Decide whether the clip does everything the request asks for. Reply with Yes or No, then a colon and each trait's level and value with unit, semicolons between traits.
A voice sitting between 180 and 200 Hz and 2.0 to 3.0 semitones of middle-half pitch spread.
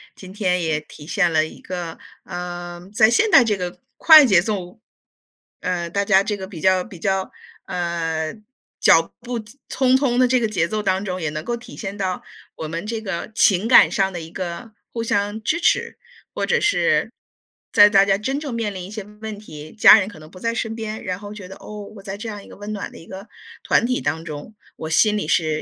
No: high, 195 Hz; average, 3.8 semitones